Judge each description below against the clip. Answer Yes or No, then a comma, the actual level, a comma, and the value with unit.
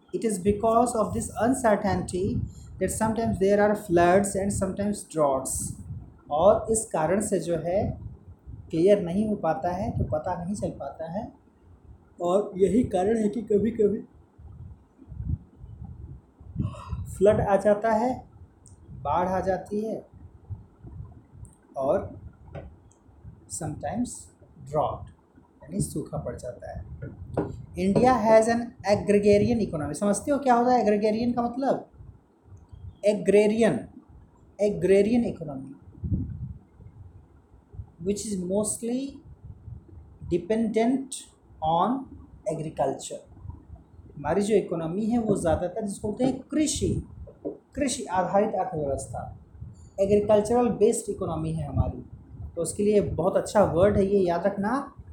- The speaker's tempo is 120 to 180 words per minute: No, slow, 110 wpm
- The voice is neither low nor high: No, high, 195 Hz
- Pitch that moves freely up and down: Yes, wide, 6.1 semitones